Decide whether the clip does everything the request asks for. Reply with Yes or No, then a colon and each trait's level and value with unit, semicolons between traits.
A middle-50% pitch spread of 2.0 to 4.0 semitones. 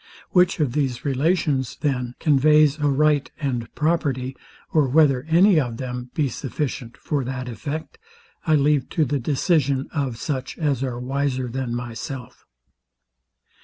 Yes: average, 3.2 semitones